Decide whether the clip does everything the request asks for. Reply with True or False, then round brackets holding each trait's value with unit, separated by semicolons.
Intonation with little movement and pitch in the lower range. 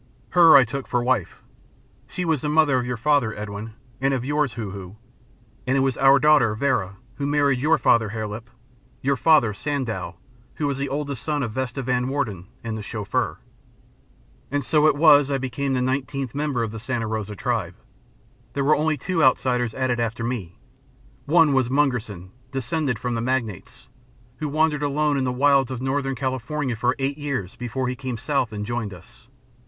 False (3.8 semitones; 130 Hz)